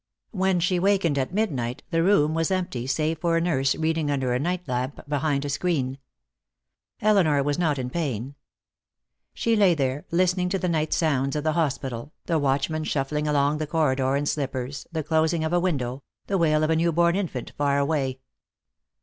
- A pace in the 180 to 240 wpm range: Yes, average, 185 wpm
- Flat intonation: No, average, 3.7 semitones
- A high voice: No, medium, 155 Hz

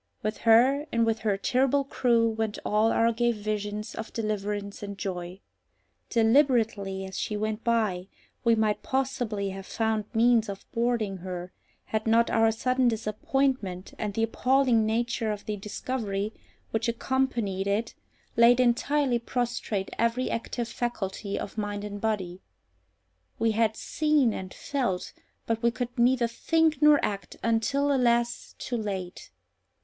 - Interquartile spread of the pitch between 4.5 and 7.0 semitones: No, average, 2.8 semitones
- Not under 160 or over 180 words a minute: No, average, 145 wpm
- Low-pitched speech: No, high, 225 Hz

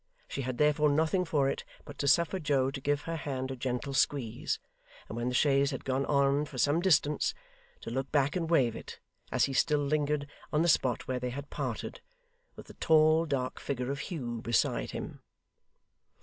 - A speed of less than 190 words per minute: No, average, 195 wpm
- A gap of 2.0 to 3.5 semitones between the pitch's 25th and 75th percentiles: Yes, narrow, 2.5 semitones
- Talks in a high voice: No, medium, 140 Hz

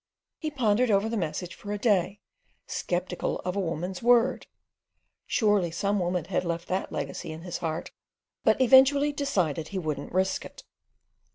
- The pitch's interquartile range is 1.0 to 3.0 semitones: No, average, 4.8 semitones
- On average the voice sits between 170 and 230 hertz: Yes, high, 190 Hz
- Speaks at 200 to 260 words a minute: No, average, 150 wpm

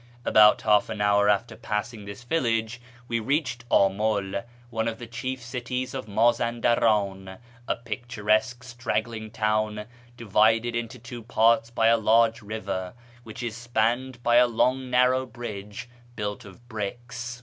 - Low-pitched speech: Yes, low, 115 Hz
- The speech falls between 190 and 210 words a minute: No, average, 140 wpm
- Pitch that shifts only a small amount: Yes, narrow, 2.1 semitones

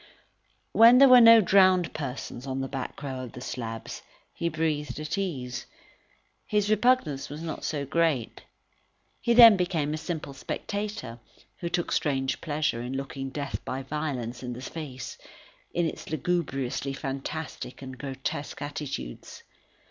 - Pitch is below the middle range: No, medium, 145 Hz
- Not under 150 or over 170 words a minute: No, average, 140 wpm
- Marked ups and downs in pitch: No, average, 4.6 semitones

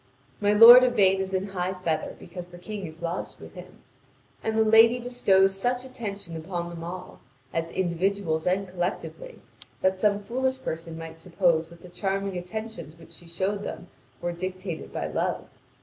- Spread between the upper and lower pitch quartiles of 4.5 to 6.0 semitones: No, average, 3.3 semitones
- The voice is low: No, high, 190 Hz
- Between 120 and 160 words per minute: No, average, 170 wpm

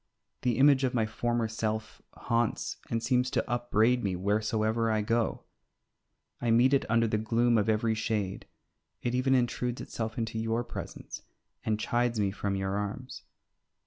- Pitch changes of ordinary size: No, narrow, 1.9 semitones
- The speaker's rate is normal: Yes, average, 160 wpm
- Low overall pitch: Yes, low, 115 Hz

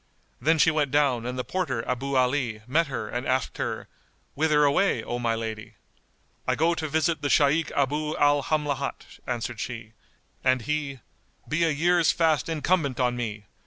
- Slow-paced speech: No, average, 170 wpm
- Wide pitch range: No, average, 3.9 semitones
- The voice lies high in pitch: No, medium, 140 Hz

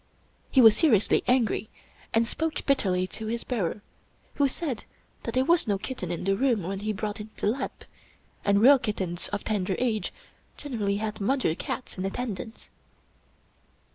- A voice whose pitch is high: Yes, high, 215 Hz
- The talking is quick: No, average, 165 wpm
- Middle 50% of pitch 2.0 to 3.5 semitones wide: No, average, 4.3 semitones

